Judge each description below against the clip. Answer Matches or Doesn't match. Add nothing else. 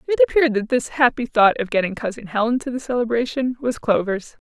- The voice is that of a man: Doesn't match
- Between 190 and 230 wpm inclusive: Matches